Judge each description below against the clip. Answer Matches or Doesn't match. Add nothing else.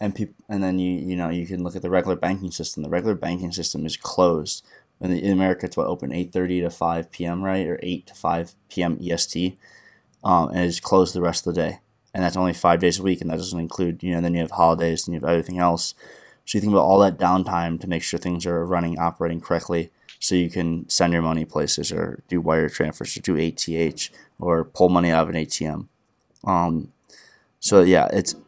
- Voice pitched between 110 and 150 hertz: Doesn't match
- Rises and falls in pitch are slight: Matches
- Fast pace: Matches